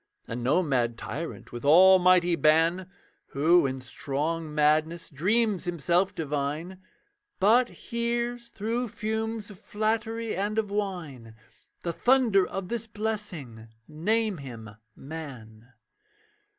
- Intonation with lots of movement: Yes, wide, 6.7 semitones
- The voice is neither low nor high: Yes, medium, 175 Hz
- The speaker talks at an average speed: No, slow, 110 wpm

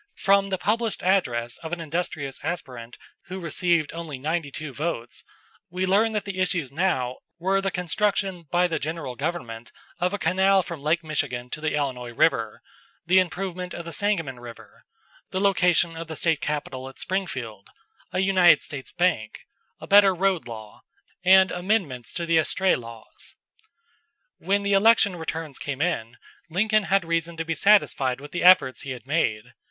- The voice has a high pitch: No, medium, 170 Hz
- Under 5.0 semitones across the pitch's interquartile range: No, average, 5.3 semitones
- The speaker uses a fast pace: No, average, 170 wpm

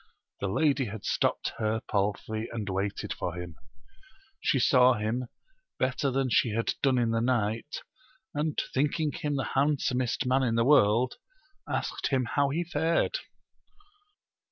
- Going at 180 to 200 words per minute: No, average, 145 wpm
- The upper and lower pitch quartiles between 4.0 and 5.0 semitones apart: Yes, average, 4.3 semitones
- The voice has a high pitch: No, low, 125 Hz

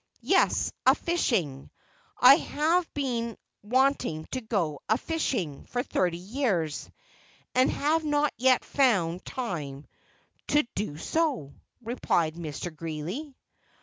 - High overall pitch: Yes, high, 230 Hz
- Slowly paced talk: Yes, slow, 115 wpm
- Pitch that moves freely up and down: Yes, wide, 9.0 semitones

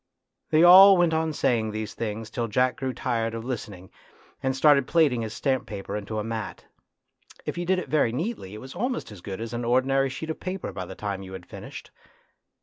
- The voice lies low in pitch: Yes, low, 125 Hz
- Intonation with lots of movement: Yes, wide, 6.3 semitones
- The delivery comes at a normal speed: No, fast, 220 wpm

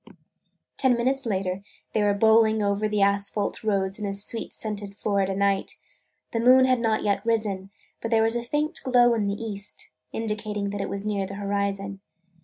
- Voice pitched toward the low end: No, high, 210 Hz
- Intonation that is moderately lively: No, narrow, 2.2 semitones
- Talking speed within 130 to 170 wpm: No, average, 185 wpm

